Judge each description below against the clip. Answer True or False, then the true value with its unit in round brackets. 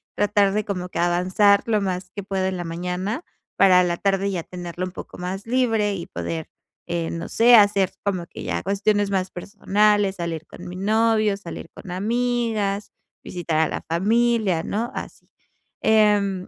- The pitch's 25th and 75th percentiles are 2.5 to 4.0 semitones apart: True (2.8 semitones)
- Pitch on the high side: True (195 Hz)